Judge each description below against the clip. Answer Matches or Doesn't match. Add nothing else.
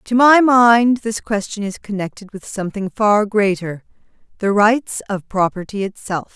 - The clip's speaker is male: Doesn't match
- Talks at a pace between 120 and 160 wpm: Matches